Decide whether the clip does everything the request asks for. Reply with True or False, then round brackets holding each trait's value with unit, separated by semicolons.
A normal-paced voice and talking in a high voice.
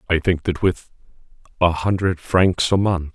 False (170 wpm; 90 Hz)